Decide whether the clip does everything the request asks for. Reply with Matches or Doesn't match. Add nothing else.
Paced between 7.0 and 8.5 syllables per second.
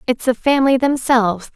Doesn't match